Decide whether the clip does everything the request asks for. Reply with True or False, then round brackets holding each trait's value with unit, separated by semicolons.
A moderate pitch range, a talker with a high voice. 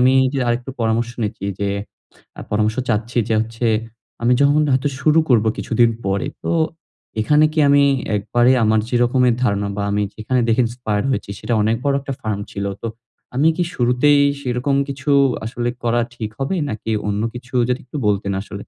False (3.2 semitones; 120 Hz)